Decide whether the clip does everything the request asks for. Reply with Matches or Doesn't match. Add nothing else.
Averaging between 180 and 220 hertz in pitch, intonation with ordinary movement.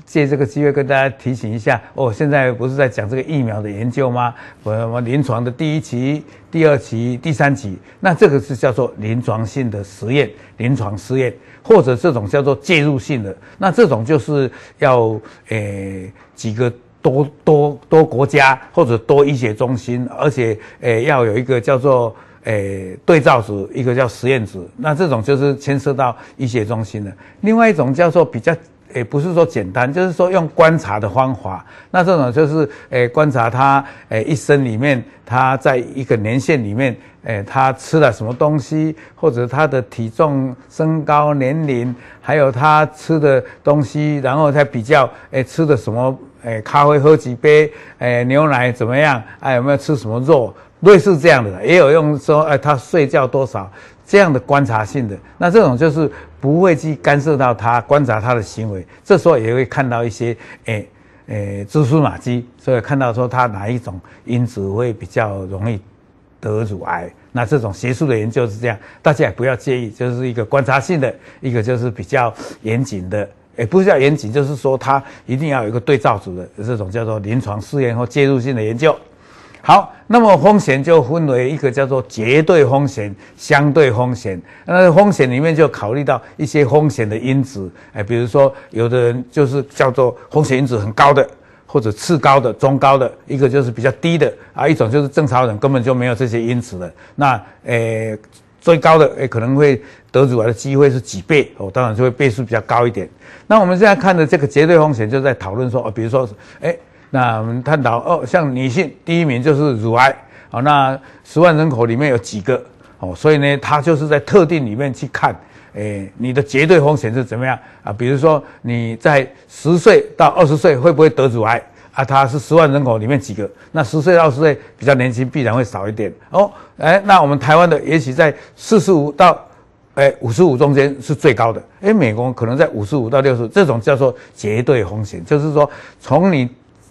Doesn't match